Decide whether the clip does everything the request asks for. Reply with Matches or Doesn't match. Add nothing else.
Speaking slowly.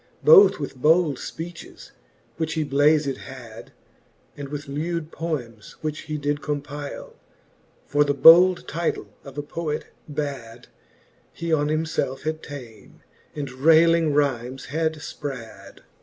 Matches